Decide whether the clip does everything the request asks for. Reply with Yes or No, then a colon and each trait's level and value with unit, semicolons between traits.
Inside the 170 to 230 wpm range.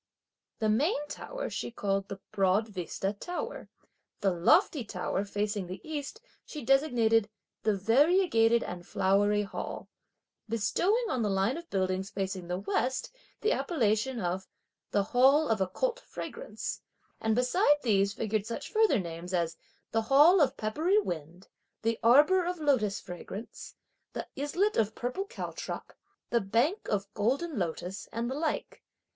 No: average, 145 wpm